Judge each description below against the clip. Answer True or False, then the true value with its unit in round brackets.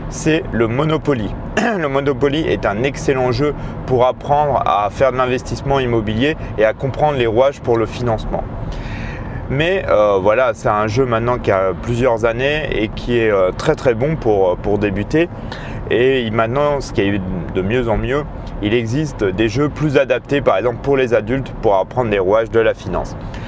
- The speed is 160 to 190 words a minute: True (185 wpm)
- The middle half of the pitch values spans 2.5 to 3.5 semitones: False (4.2 semitones)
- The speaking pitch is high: False (125 Hz)